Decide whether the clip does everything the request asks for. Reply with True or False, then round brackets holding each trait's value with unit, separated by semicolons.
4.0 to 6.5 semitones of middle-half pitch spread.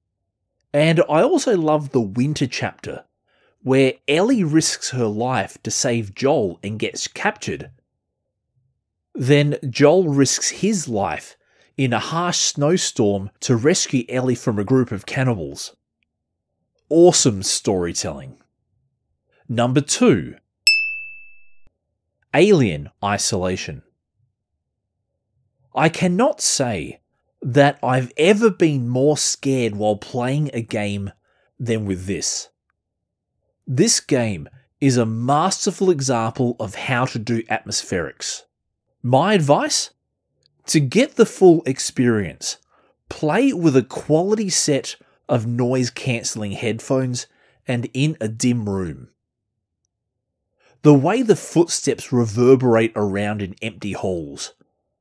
True (5.4 semitones)